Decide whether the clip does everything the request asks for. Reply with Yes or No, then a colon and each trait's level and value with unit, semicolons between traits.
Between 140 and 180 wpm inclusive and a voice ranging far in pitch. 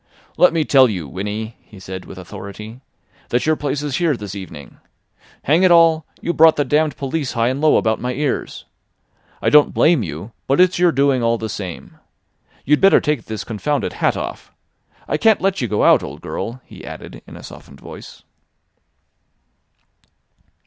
Yes: average, 175 wpm; wide, 6.4 semitones